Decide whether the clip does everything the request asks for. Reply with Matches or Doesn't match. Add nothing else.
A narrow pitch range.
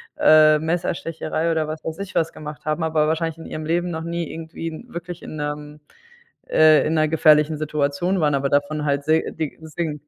Matches